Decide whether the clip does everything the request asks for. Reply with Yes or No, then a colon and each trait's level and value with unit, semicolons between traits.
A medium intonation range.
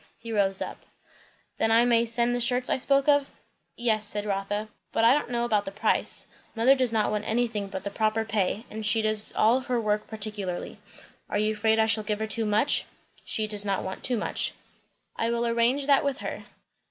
No: narrow, 2.1 semitones